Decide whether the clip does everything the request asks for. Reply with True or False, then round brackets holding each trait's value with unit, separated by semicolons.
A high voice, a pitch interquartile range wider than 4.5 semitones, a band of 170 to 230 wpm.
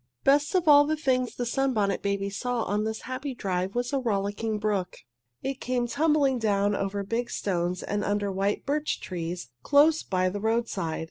True (220 Hz; 4.9 semitones; 180 wpm)